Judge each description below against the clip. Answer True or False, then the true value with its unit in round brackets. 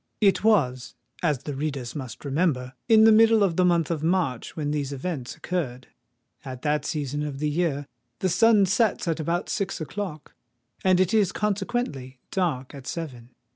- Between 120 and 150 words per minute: False (175 wpm)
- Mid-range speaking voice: True (160 Hz)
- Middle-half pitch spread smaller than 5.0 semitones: False (5.5 semitones)